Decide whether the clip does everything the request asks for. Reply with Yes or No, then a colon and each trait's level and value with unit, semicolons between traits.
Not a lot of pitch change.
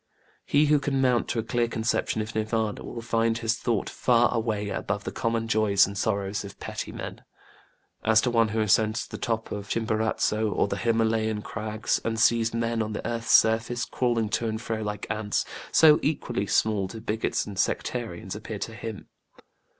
Yes: narrow, 1.4 semitones